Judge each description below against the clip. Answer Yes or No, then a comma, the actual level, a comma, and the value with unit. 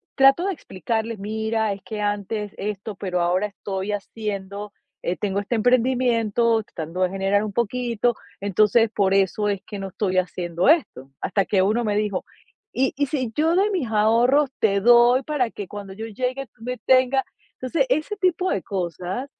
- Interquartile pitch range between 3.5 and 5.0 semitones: Yes, average, 4.1 semitones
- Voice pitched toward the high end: Yes, high, 215 Hz